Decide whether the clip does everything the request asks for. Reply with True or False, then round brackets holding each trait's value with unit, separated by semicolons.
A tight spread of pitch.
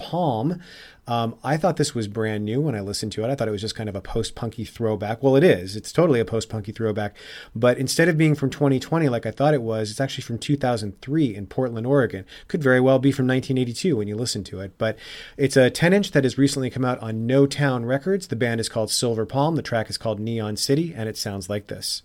False (4.1 semitones)